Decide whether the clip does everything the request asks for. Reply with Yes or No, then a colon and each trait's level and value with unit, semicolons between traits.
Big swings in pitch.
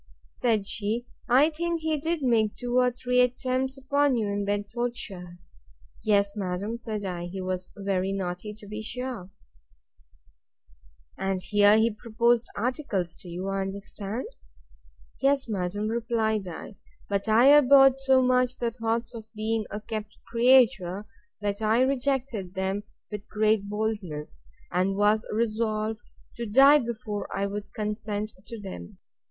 No: average, 3.5 semitones